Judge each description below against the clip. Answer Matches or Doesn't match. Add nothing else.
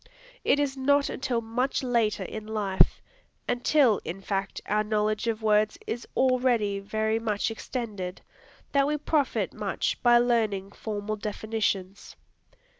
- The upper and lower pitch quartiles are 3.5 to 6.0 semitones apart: Doesn't match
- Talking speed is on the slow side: Matches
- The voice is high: Matches